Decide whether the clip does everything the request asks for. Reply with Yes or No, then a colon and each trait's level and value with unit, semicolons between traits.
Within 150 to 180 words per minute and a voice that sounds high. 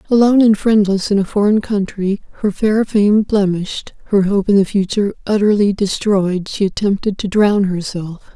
Yes: average, 165 wpm; high, 200 Hz